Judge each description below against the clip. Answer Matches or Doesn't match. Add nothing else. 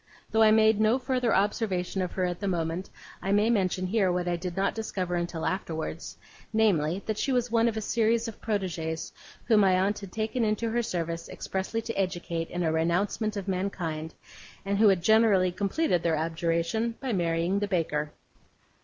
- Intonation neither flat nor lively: Matches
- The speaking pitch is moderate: Doesn't match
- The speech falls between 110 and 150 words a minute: Doesn't match